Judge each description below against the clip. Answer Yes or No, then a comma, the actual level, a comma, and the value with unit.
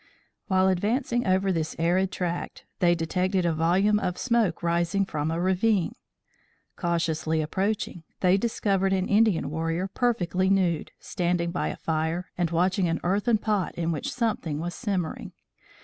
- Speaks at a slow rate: No, average, 150 wpm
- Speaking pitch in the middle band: Yes, medium, 180 Hz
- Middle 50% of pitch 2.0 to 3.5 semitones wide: Yes, average, 2.8 semitones